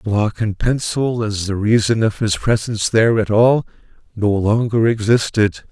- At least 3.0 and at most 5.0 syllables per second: Yes, 4.5 syllables/s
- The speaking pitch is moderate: No, low, 110 Hz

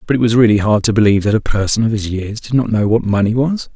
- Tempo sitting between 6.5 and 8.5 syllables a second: Yes, 6.7 syllables/s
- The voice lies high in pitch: No, low, 110 Hz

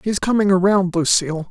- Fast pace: No, average, 160 wpm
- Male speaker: No, female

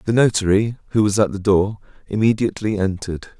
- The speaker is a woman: No, male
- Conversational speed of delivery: Yes, average, 160 wpm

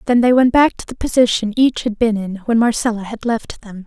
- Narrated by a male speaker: No, female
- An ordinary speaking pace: No, fast, 250 wpm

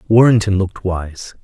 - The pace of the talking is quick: No, slow, 125 wpm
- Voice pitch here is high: No, low, 100 Hz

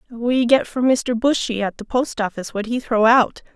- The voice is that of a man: No, female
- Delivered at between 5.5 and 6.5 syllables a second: No, 5.0 syllables/s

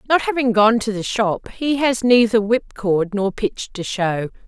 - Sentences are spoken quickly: No, average, 190 wpm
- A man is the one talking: No, female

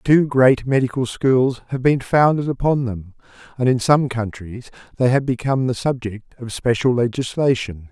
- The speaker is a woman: No, male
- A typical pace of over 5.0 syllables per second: No, 4.7 syllables/s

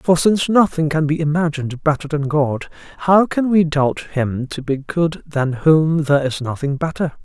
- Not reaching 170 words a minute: No, average, 190 wpm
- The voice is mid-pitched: Yes, medium, 155 Hz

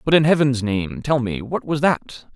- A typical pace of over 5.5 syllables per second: No, 4.5 syllables/s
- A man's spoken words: Yes, male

